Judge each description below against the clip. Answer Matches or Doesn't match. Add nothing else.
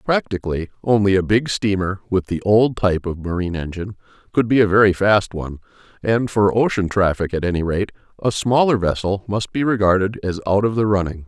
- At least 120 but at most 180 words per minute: Doesn't match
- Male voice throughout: Matches